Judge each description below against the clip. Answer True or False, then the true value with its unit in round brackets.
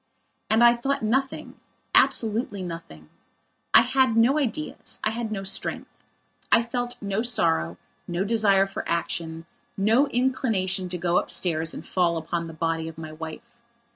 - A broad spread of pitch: True (6.1 semitones)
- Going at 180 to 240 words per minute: False (150 wpm)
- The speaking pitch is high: True (195 Hz)